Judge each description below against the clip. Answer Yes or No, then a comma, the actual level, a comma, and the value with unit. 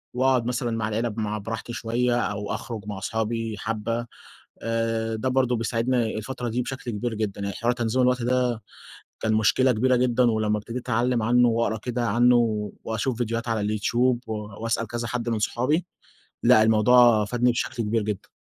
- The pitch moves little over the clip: Yes, narrow, 2.0 semitones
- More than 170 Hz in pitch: No, low, 115 Hz